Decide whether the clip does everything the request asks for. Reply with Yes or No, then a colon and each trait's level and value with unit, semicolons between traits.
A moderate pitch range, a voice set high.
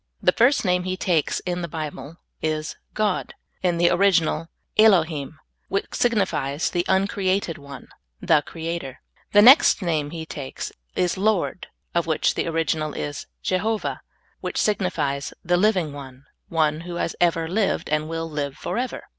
No: average, 3.6 semitones; medium, 170 Hz